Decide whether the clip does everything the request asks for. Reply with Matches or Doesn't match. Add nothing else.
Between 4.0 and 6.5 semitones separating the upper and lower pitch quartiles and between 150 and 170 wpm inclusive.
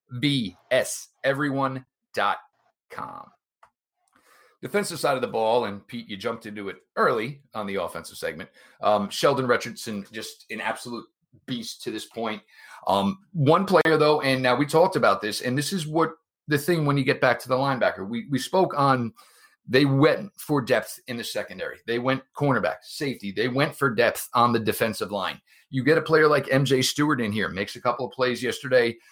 Doesn't match